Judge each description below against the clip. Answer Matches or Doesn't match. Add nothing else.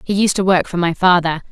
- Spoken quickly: Matches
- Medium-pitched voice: Matches